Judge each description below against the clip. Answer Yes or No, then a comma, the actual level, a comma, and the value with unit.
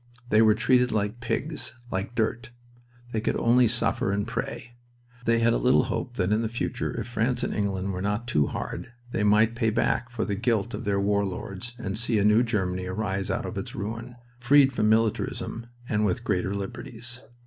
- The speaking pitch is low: Yes, low, 110 Hz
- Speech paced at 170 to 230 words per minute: Yes, average, 200 wpm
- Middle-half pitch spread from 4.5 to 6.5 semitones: No, average, 2.9 semitones